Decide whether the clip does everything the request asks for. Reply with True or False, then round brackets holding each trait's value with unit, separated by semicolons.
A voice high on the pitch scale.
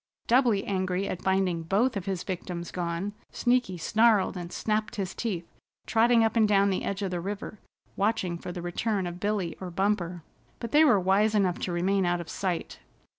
True (195 Hz)